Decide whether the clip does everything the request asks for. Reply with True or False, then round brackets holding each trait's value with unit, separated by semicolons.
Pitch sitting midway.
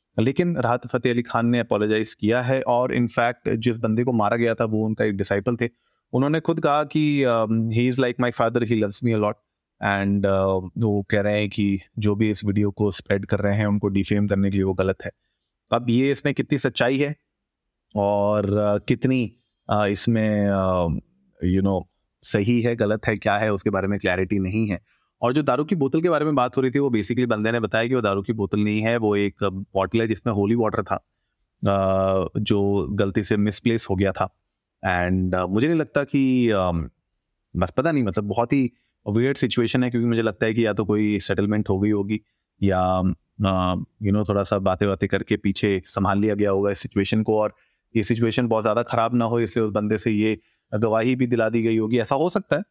False (110 Hz)